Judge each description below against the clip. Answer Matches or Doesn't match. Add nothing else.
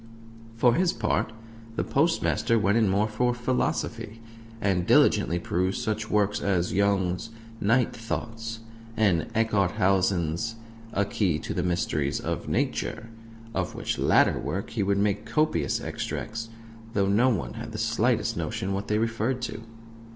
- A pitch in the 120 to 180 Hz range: Doesn't match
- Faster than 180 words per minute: Doesn't match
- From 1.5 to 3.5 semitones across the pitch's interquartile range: Matches